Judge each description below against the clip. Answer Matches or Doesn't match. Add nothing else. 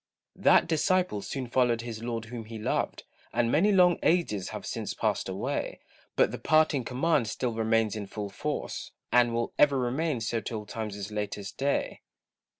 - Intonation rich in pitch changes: Doesn't match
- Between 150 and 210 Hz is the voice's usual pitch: Doesn't match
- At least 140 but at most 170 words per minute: Matches